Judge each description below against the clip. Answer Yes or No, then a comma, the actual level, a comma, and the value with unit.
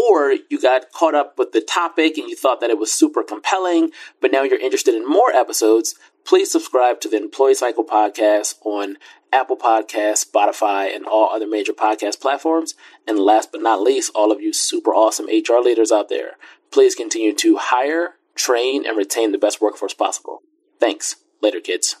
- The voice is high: Yes, very high, 315 Hz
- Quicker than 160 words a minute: Yes, average, 185 wpm